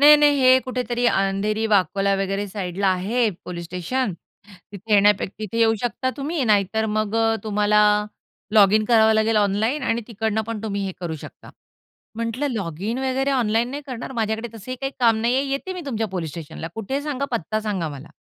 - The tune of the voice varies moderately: Yes, average, 3.9 semitones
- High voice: Yes, high, 220 Hz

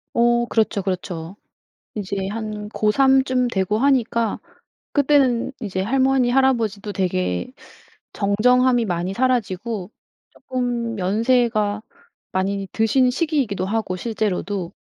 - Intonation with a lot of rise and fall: No, average, 4.1 semitones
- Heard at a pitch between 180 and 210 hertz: No, high, 220 Hz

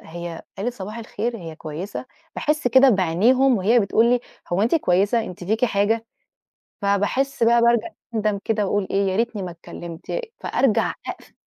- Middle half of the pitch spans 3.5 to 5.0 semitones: Yes, average, 4.0 semitones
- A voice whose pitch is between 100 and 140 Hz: No, high, 210 Hz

